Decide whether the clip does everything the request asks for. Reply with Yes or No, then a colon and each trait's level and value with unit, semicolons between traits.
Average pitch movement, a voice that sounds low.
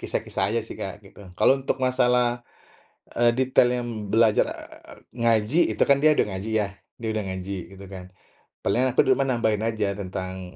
Yes: average, 3.9 semitones; low, 110 Hz